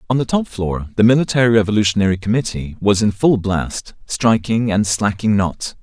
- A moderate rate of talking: Yes, average, 165 wpm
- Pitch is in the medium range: No, low, 105 Hz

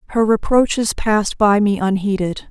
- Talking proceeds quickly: No, average, 145 wpm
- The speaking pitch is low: No, high, 210 Hz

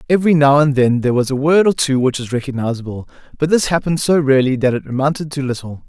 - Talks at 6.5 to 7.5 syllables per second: Yes, 6.9 syllables/s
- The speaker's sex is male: Yes, male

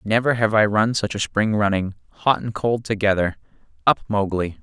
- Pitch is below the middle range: Yes, low, 105 Hz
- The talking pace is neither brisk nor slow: Yes, average, 170 wpm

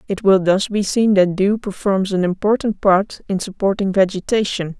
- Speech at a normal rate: Yes, average, 175 wpm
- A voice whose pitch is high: Yes, high, 195 Hz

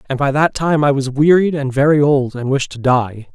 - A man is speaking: Yes, male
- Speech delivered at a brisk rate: Yes, fast, 250 wpm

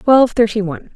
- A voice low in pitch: No, high, 215 Hz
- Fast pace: No, average, 190 wpm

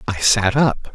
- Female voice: No, male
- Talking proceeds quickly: No, average, 190 wpm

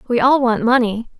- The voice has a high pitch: Yes, high, 240 Hz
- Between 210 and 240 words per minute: No, average, 200 wpm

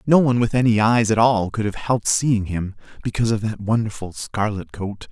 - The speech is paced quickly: Yes, fast, 210 wpm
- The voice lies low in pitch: Yes, low, 110 Hz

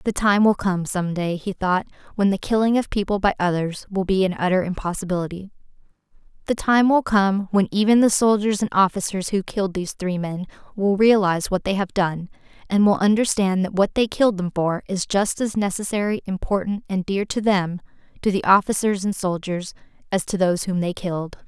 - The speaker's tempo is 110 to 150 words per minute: No, average, 190 wpm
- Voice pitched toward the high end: Yes, high, 195 Hz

